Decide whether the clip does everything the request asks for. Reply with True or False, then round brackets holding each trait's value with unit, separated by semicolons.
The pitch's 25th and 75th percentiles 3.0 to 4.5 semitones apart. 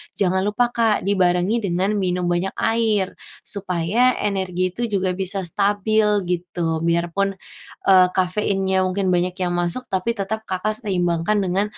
False (2.6 semitones)